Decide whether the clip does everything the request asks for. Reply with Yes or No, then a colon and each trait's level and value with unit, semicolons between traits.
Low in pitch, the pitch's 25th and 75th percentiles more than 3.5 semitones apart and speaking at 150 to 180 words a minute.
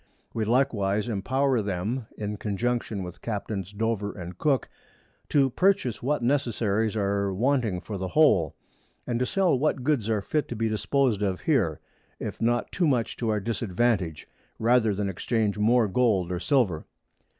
Yes: low, 110 Hz; average, 4.0 semitones; average, 160 wpm